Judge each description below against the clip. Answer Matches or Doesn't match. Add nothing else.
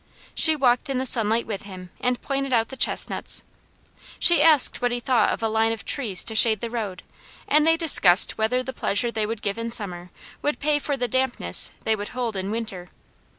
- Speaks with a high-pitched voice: Matches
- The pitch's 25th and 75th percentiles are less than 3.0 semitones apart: Doesn't match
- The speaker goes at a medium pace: Doesn't match